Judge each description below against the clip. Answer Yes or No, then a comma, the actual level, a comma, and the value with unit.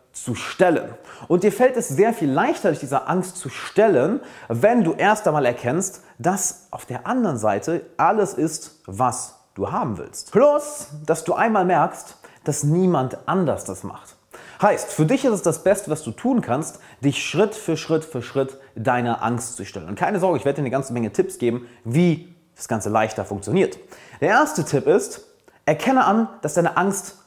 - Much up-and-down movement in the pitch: Yes, wide, 7.5 semitones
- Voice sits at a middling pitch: Yes, medium, 160 Hz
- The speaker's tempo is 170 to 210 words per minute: Yes, fast, 190 wpm